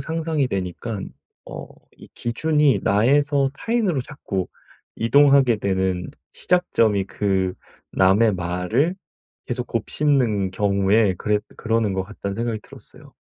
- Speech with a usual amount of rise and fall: No, wide, 6.3 semitones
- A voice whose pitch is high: No, low, 115 Hz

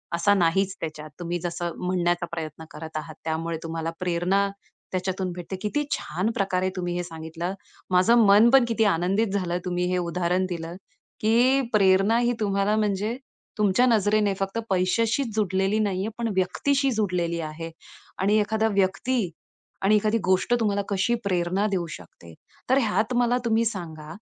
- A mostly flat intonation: No, average, 3.6 semitones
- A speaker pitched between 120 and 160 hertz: No, high, 190 Hz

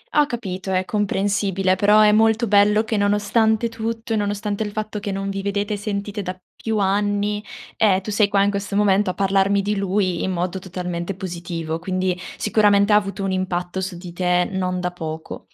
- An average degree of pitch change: No, narrow, 1.9 semitones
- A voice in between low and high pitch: No, high, 200 Hz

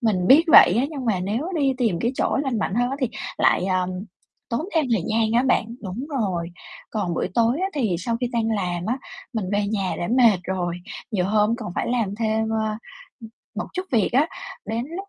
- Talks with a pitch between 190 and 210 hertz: No, high, 220 Hz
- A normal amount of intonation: Yes, average, 4.3 semitones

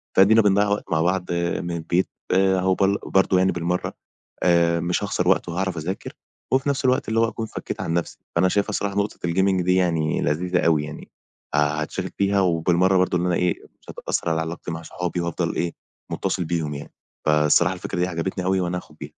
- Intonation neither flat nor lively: No, narrow, 2.3 semitones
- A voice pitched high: No, very low, 90 Hz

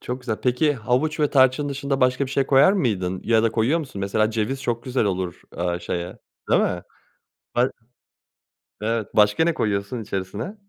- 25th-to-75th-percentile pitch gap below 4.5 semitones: No, average, 4.9 semitones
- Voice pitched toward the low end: Yes, low, 120 Hz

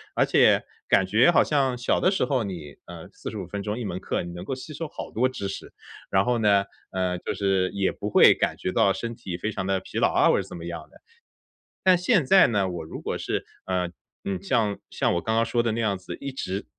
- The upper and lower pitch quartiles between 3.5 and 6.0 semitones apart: Yes, average, 4.8 semitones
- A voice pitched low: Yes, low, 100 Hz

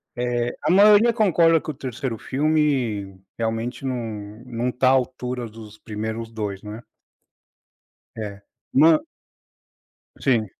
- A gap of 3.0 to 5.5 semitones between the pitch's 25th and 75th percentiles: Yes, average, 4.0 semitones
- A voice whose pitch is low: Yes, low, 120 Hz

